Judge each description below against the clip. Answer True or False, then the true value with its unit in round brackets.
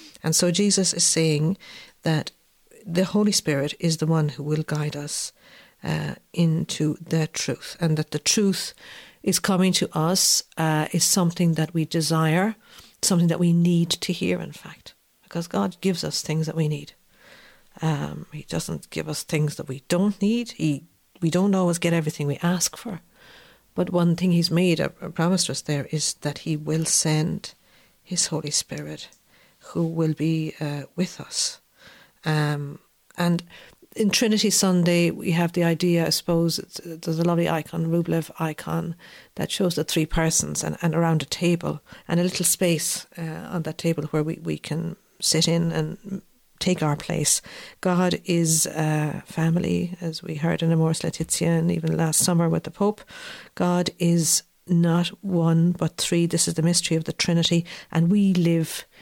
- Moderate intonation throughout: False (2.2 semitones)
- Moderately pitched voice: True (170 Hz)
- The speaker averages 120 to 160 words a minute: False (175 wpm)